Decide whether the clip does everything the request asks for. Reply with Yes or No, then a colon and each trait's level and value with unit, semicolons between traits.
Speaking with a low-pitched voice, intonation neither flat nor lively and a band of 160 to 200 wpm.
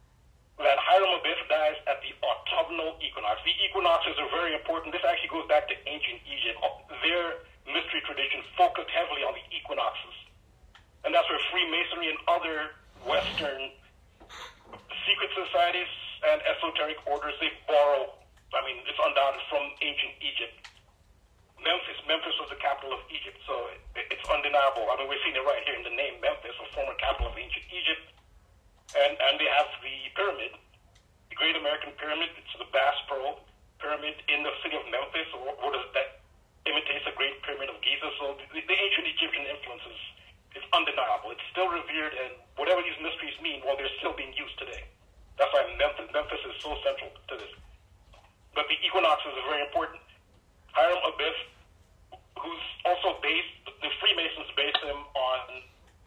No: medium, 150 Hz; average, 4.0 semitones; average, 165 wpm